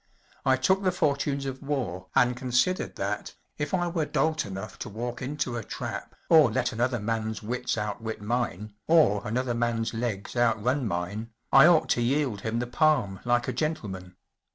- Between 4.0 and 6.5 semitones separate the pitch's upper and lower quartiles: Yes, average, 4.4 semitones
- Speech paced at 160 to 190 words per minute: Yes, average, 175 wpm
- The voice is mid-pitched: No, low, 120 Hz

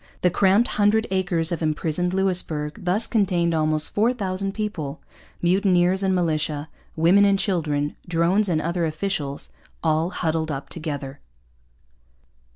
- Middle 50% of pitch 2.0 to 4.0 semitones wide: Yes, average, 3.6 semitones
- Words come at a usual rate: No, slow, 125 wpm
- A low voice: No, medium, 175 Hz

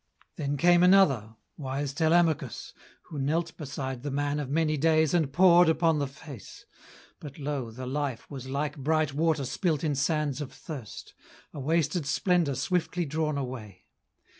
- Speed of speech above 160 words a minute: No, average, 155 wpm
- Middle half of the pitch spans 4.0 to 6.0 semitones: No, average, 2.9 semitones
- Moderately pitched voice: Yes, medium, 145 Hz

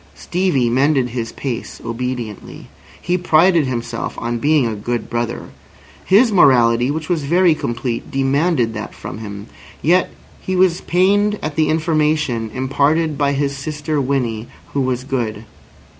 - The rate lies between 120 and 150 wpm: Yes, average, 145 wpm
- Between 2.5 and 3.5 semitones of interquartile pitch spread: No, average, 5.1 semitones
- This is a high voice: No, medium, 140 Hz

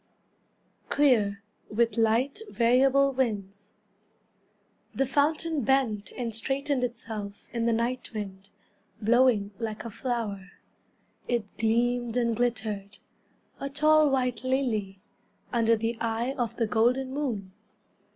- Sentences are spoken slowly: Yes, slow, 110 wpm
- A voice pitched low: No, high, 235 Hz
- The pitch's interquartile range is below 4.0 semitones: Yes, average, 3.3 semitones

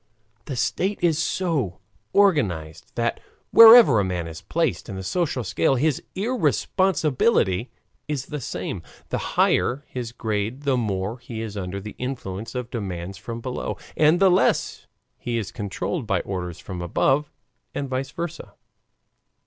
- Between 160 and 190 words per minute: No, average, 150 wpm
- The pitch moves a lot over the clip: Yes, wide, 7.5 semitones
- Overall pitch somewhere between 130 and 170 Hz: No, low, 120 Hz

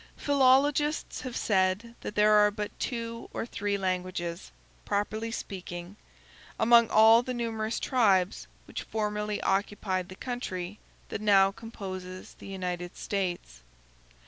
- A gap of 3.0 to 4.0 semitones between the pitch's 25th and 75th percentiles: Yes, average, 3.5 semitones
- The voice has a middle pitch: No, high, 210 Hz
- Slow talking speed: Yes, slow, 120 wpm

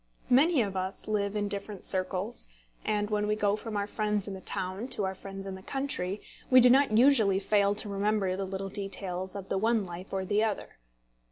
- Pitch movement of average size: No, narrow, 1.9 semitones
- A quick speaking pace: Yes, fast, 210 wpm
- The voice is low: No, high, 200 Hz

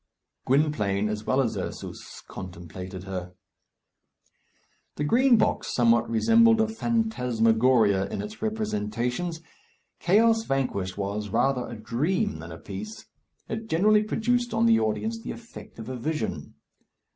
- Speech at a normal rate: No, slow, 130 wpm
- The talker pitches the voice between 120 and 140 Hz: Yes, low, 135 Hz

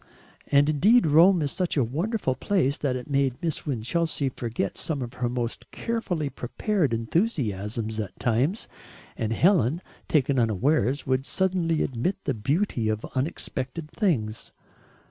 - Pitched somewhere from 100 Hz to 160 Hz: Yes, medium, 140 Hz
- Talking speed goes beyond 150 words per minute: No, average, 140 wpm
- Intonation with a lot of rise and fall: Yes, wide, 5.9 semitones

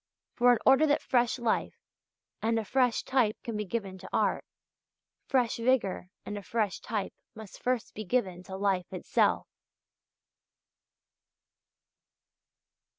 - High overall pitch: Yes, high, 225 Hz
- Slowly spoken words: Yes, slow, 130 wpm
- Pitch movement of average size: Yes, average, 3.9 semitones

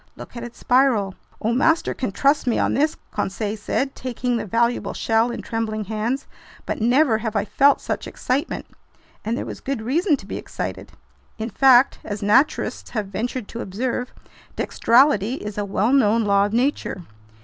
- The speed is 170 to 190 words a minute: Yes, average, 175 wpm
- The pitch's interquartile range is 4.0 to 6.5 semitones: No, average, 3.6 semitones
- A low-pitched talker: No, high, 235 Hz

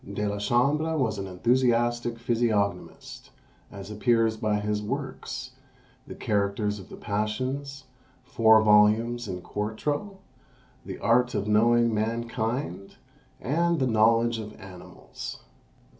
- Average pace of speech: No, slow, 115 wpm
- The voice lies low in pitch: Yes, low, 110 Hz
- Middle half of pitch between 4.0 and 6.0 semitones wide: No, average, 2.7 semitones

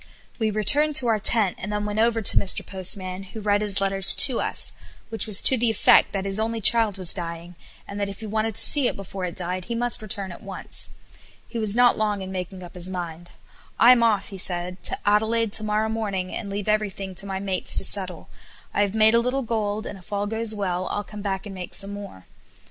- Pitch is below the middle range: No, high, 205 Hz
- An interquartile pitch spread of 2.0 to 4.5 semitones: Yes, narrow, 2.6 semitones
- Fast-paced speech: Yes, fast, 235 wpm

